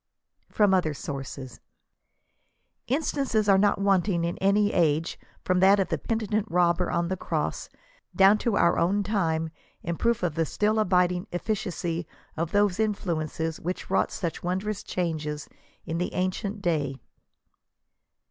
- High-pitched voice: No, medium, 180 Hz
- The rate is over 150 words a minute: No, average, 145 wpm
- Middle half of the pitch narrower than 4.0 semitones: Yes, average, 3.6 semitones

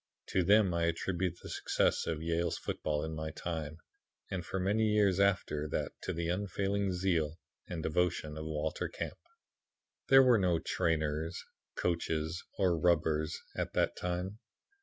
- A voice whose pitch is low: Yes, very low, 85 Hz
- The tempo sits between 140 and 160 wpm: Yes, average, 150 wpm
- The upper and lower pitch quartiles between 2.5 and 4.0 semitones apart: Yes, average, 3.2 semitones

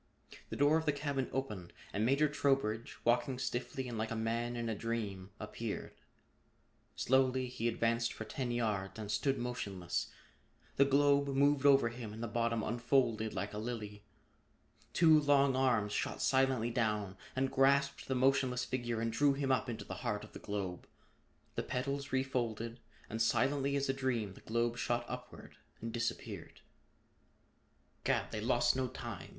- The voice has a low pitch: Yes, low, 120 Hz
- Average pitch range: Yes, average, 3.1 semitones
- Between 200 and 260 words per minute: No, average, 165 wpm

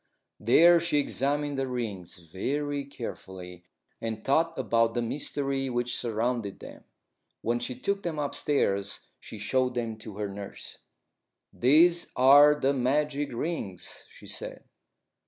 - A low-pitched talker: Yes, low, 125 Hz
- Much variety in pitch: No, average, 4.8 semitones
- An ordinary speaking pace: No, slow, 130 wpm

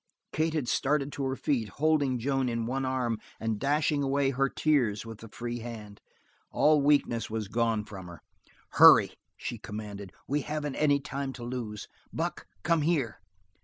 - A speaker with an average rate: Yes, average, 165 wpm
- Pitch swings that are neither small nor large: Yes, average, 4.1 semitones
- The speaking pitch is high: No, low, 130 Hz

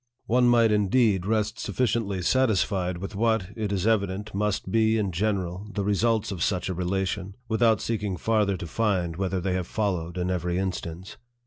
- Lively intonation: No, average, 3.1 semitones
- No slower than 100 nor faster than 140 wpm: No, average, 175 wpm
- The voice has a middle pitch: No, low, 100 Hz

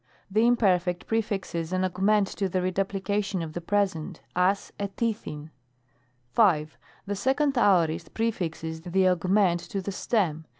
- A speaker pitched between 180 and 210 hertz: Yes, high, 190 Hz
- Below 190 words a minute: Yes, average, 140 wpm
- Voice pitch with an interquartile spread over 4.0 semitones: No, average, 3.1 semitones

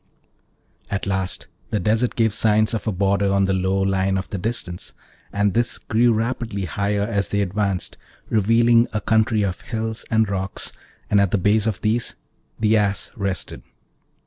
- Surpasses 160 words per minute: Yes, average, 170 wpm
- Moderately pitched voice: No, low, 105 Hz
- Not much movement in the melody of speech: Yes, narrow, 2.3 semitones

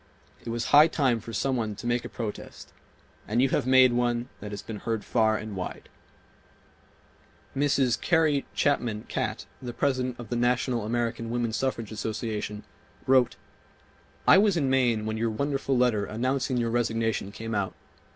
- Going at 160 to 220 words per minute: Yes, average, 170 wpm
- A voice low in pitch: Yes, low, 120 Hz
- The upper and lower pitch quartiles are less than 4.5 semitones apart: Yes, average, 2.8 semitones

